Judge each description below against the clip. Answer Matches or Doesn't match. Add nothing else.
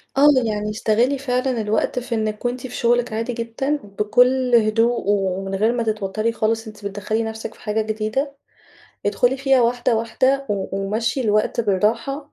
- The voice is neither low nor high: Doesn't match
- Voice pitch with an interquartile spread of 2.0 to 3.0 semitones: Matches